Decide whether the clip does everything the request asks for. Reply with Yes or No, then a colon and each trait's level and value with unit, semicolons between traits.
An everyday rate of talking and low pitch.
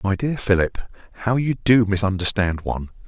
Yes: average, 155 wpm; low, 105 Hz